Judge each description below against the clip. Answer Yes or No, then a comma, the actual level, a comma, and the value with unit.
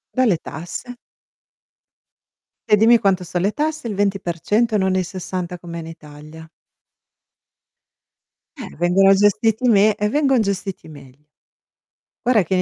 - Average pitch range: Yes, average, 4.0 semitones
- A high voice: Yes, high, 195 Hz